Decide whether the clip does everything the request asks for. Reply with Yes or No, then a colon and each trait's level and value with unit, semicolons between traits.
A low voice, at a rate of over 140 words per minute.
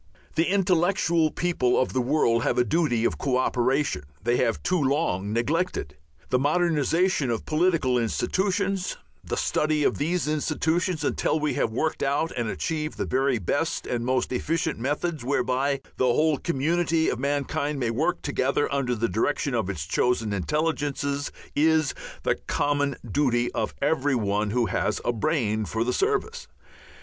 No: medium, 145 Hz; average, 160 wpm